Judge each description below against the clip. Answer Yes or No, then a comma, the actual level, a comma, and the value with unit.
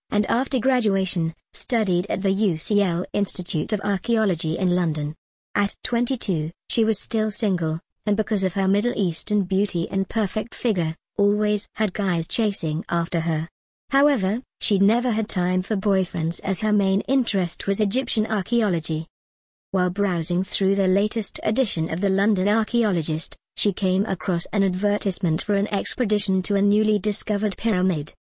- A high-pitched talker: Yes, high, 200 Hz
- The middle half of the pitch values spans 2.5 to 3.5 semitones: Yes, average, 3.1 semitones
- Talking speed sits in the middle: Yes, average, 150 wpm